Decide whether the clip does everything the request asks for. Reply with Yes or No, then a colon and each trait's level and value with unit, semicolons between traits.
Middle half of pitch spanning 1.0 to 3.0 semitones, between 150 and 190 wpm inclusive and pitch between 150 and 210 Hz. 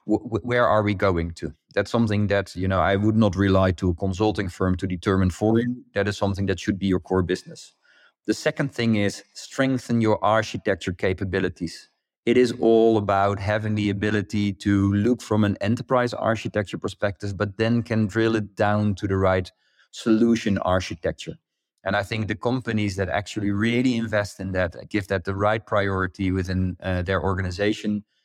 No: narrow, 2.5 semitones; average, 180 wpm; low, 105 Hz